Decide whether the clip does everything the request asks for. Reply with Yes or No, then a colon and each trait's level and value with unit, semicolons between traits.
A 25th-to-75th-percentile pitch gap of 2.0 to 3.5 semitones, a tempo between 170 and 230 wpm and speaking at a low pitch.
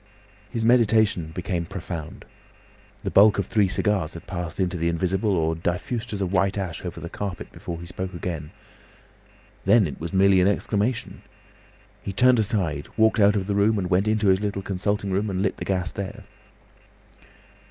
Yes: average, 2.9 semitones; average, 180 wpm; very low, 95 Hz